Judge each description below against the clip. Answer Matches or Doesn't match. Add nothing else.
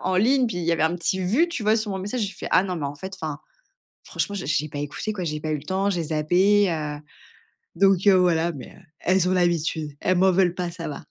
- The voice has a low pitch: Doesn't match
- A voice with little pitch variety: Doesn't match